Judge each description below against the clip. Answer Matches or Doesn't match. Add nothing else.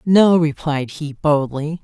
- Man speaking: Doesn't match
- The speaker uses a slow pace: Matches